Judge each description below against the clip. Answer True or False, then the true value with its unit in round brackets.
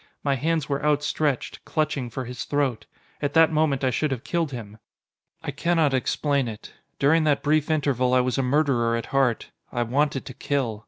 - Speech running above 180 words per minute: True (190 wpm)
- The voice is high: False (140 Hz)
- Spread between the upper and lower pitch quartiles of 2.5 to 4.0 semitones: True (3.3 semitones)